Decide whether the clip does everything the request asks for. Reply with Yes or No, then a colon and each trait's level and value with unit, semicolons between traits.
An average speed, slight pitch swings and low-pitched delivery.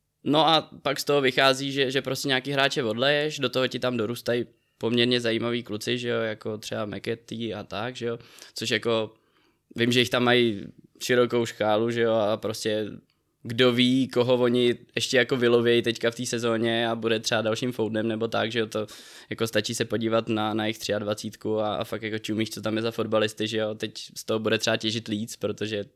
No: fast, 210 wpm; narrow, 2.0 semitones; low, 115 Hz